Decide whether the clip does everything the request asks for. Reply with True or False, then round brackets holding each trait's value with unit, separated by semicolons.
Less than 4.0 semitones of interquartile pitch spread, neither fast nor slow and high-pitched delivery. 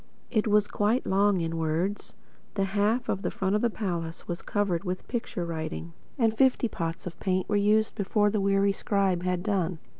True (3.1 semitones; 180 wpm; 195 Hz)